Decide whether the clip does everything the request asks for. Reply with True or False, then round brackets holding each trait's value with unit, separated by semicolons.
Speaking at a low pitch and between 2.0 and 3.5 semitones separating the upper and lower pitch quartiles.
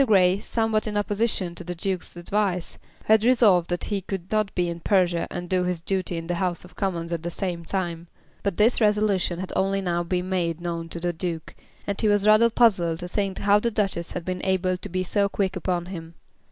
False (185 Hz; 2.9 semitones)